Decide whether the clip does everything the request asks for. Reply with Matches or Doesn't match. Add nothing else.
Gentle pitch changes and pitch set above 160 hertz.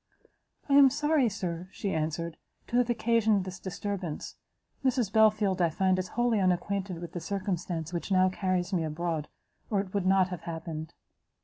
Doesn't match